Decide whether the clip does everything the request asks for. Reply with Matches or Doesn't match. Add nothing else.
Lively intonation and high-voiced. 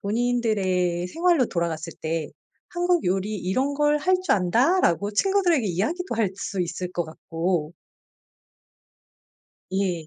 Matches